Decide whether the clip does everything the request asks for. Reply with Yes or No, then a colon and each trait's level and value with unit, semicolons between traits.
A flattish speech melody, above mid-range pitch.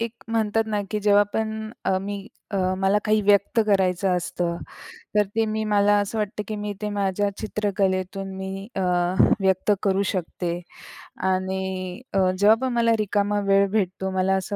Yes: narrow, 1.8 semitones; high, 200 Hz